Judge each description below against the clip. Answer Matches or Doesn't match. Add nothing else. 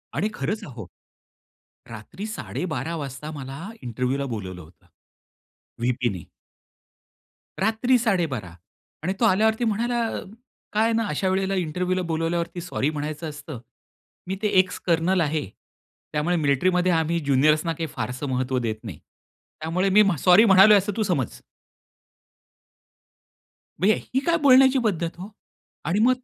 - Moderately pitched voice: Matches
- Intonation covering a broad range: Matches